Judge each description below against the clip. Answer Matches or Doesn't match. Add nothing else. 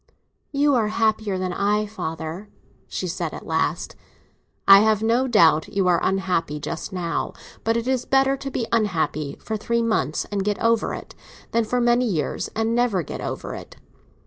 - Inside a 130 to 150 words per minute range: Doesn't match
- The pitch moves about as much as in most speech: Matches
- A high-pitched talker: Matches